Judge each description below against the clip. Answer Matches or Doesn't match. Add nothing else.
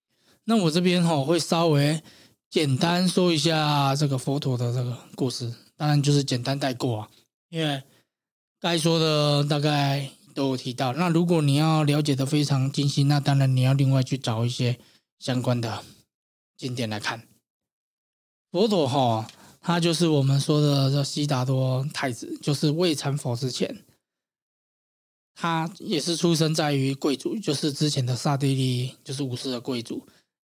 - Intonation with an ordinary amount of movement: Matches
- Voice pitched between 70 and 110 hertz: Doesn't match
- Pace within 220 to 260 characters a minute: Matches